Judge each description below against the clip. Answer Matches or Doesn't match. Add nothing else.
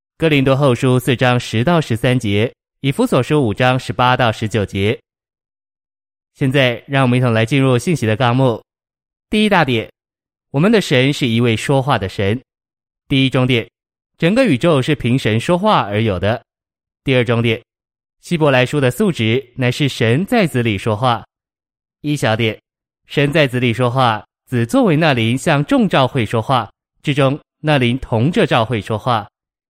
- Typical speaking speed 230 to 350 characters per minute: Matches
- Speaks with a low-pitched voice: Matches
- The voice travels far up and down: Doesn't match